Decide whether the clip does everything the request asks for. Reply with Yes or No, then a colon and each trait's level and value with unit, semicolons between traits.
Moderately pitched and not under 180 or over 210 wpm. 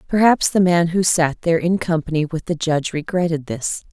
Yes: medium, 170 Hz; average, 200 wpm